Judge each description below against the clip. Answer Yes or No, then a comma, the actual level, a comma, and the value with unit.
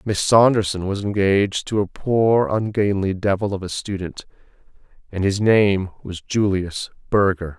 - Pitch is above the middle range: No, low, 100 Hz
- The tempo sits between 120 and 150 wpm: Yes, average, 140 wpm